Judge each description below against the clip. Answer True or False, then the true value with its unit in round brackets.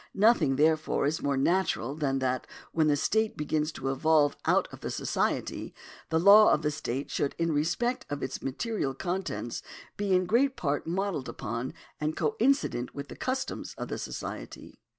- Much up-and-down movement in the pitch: True (5.7 semitones)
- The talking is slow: False (170 wpm)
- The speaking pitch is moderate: True (155 Hz)